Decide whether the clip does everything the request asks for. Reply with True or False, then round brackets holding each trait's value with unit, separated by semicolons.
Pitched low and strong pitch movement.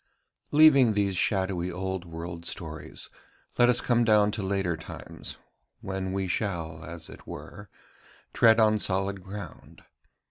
False (95 Hz; 3.5 semitones)